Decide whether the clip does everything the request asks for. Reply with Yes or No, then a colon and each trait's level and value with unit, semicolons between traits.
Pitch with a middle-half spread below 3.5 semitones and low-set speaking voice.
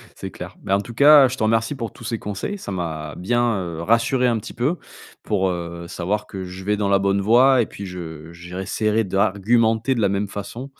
No: average, 4.0 semitones; low, 105 Hz